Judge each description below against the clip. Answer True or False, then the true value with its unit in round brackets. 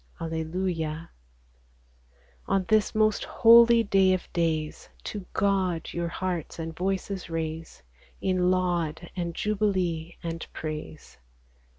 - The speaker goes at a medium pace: False (105 wpm)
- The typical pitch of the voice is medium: True (175 Hz)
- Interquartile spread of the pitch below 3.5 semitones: True (3.0 semitones)